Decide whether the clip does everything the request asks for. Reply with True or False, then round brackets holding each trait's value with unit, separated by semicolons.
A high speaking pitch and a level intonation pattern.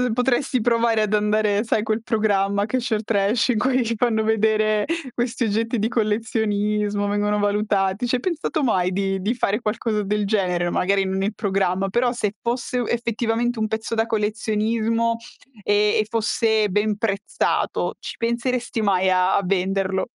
True (215 Hz; 2.3 semitones)